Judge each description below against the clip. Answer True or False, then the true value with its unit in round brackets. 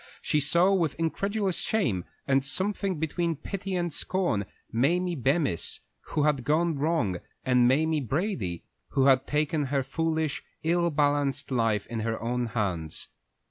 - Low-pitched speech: False (150 Hz)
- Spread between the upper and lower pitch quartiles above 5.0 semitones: True (5.4 semitones)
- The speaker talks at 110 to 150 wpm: True (140 wpm)